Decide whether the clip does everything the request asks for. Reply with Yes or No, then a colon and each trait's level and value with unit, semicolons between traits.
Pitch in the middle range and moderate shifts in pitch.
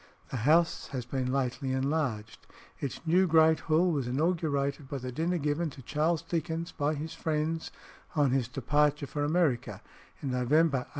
Yes: medium, 150 Hz; average, 3.5 semitones